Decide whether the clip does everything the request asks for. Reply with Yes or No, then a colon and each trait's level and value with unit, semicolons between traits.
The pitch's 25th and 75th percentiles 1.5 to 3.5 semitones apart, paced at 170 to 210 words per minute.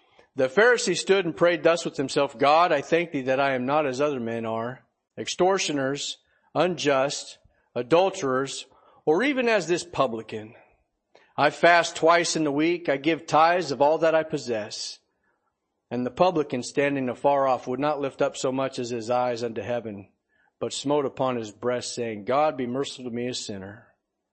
No: average, 4.6 semitones; average, 180 wpm